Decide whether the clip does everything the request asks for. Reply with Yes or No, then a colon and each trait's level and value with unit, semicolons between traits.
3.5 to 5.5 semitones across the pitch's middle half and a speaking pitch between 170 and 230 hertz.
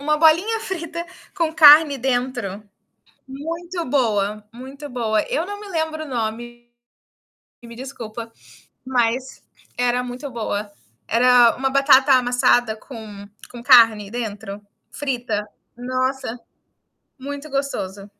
No: average, 3.9 semitones; very high, 250 Hz